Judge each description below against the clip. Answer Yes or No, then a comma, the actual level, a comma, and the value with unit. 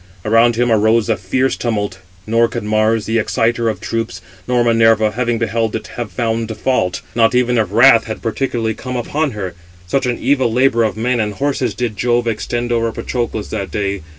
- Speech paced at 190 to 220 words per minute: Yes, average, 195 wpm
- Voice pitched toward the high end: No, low, 115 Hz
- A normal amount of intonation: No, narrow, 1.9 semitones